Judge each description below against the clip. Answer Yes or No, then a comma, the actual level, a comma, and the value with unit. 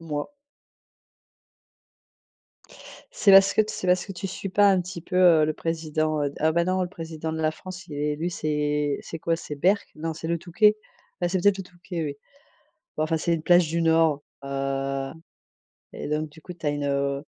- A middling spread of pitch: Yes, average, 3.2 semitones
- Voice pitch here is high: No, medium, 165 Hz